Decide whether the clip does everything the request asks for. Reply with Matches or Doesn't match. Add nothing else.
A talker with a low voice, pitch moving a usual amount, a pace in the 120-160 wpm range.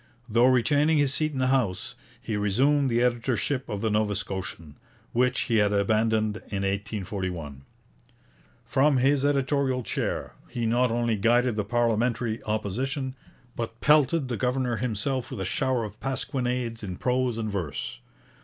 Matches